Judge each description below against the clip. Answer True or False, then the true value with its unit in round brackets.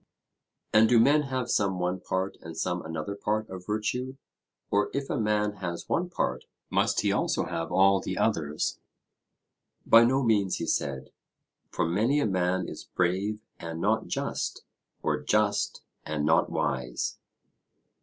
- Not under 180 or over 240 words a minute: False (155 wpm)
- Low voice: True (100 Hz)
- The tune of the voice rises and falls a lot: False (4.4 semitones)